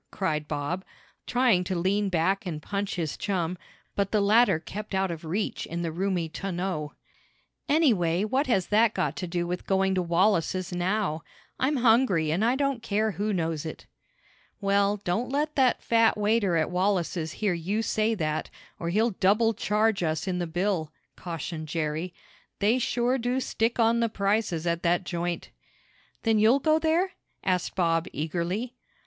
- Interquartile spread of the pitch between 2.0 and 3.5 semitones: No, average, 4.5 semitones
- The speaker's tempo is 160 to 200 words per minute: Yes, average, 165 wpm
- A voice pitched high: Yes, high, 195 Hz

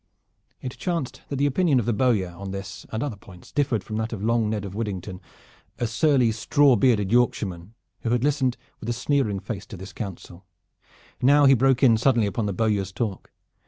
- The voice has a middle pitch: No, low, 115 Hz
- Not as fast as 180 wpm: No, average, 195 wpm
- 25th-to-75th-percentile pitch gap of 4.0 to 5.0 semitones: Yes, average, 4.6 semitones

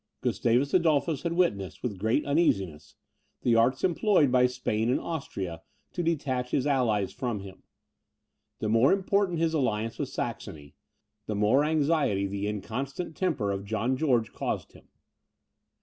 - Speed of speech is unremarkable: Yes, average, 145 wpm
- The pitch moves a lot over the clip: Yes, wide, 6.8 semitones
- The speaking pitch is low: Yes, low, 125 Hz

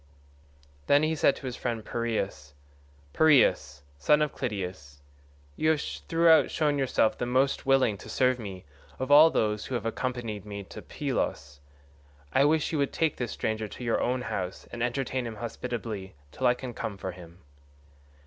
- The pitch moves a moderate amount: Yes, average, 4.9 semitones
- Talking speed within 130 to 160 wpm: No, average, 170 wpm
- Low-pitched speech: Yes, low, 120 Hz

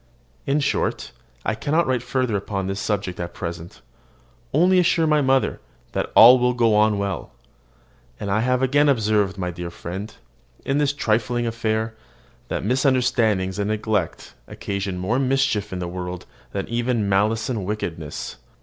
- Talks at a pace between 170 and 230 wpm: No, average, 155 wpm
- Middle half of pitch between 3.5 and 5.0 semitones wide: Yes, average, 4.7 semitones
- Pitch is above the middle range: No, low, 110 Hz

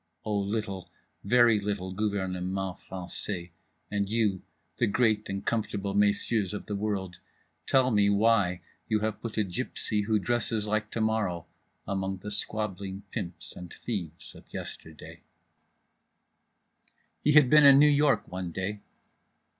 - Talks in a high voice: No, low, 105 Hz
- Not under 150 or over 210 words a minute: No, average, 140 wpm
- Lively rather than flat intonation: No, narrow, 2.5 semitones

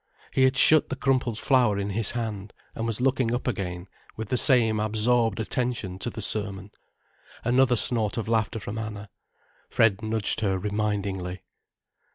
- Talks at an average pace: Yes, average, 160 wpm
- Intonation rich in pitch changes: No, average, 3.2 semitones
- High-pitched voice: No, low, 110 Hz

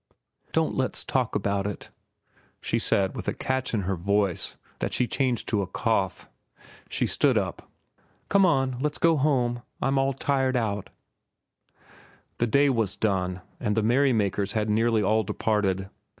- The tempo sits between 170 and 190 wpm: No, average, 155 wpm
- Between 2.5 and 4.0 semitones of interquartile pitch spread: No, average, 4.7 semitones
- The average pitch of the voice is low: Yes, low, 110 Hz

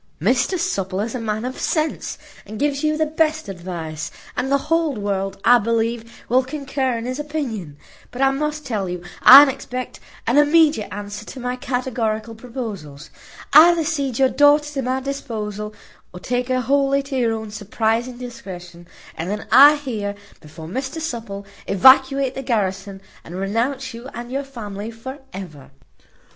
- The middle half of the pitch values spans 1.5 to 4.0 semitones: No, average, 5.0 semitones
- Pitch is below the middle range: No, high, 245 Hz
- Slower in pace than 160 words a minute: No, average, 165 wpm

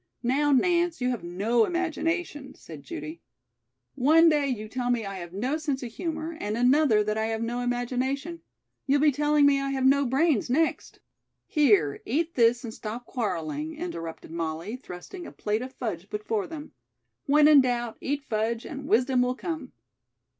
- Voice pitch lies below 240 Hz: No, very high, 255 Hz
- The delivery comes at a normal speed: Yes, average, 175 wpm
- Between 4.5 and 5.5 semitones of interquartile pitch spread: Yes, average, 5.2 semitones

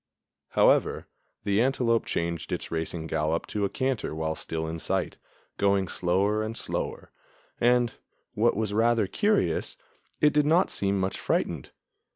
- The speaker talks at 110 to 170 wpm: Yes, average, 145 wpm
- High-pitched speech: No, low, 100 Hz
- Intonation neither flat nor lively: No, wide, 5.9 semitones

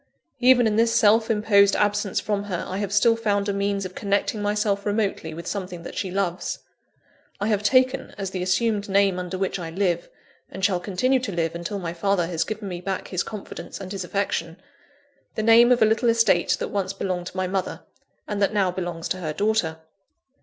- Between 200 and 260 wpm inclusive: Yes, fast, 205 wpm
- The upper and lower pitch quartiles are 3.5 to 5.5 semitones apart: No, narrow, 2.6 semitones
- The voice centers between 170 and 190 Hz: No, high, 200 Hz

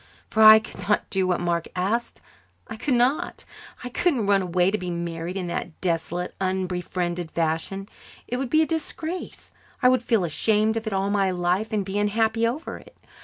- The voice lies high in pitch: Yes, high, 195 Hz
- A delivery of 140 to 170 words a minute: No, average, 190 wpm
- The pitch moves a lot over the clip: No, average, 4.2 semitones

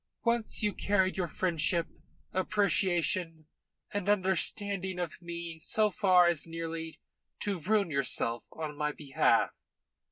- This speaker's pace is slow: Yes, slow, 120 wpm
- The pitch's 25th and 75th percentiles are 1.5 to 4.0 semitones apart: Yes, average, 3.4 semitones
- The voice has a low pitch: No, medium, 175 Hz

